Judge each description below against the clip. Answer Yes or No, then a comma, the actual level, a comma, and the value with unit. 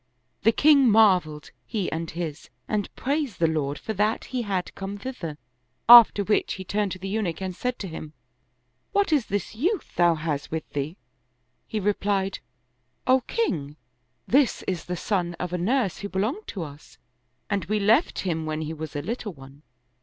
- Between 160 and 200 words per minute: Yes, average, 190 wpm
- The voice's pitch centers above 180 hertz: Yes, high, 190 Hz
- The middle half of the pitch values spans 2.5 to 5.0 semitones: No, wide, 5.5 semitones